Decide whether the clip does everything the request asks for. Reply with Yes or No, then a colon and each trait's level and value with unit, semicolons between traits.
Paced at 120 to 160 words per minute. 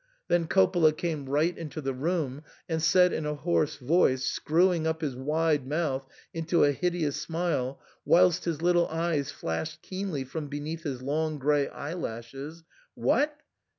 Yes: average, 155 wpm